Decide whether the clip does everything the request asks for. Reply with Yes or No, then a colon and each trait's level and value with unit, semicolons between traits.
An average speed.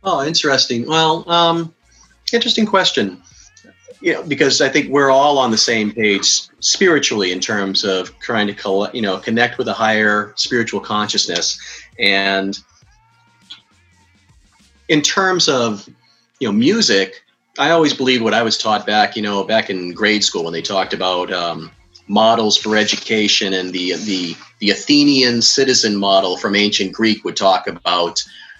Yes: average, 155 wpm